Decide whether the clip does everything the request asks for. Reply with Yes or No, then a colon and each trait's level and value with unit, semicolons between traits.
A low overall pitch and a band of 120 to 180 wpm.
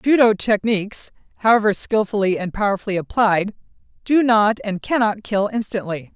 No: high, 210 Hz; slow, 135 wpm